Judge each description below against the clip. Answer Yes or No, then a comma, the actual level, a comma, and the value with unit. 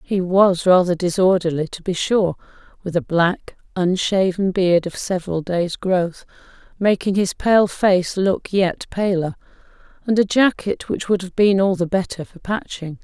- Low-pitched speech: No, medium, 185 Hz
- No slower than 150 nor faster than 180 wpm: Yes, average, 160 wpm